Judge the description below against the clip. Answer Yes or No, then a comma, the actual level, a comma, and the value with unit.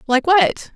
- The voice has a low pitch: No, very high, 305 Hz